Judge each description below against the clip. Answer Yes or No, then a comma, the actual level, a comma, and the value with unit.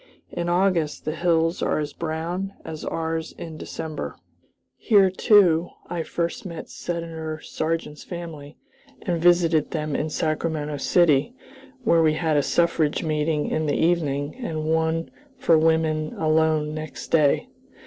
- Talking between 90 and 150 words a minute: Yes, average, 140 wpm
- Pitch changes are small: Yes, narrow, 1.6 semitones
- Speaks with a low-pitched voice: No, medium, 160 Hz